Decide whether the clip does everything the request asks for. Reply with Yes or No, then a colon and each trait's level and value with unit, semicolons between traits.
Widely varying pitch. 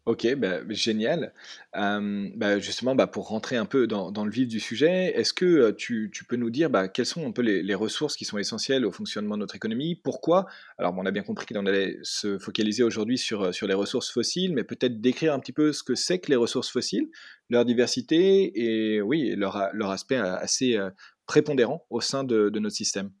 Yes: wide, 6.4 semitones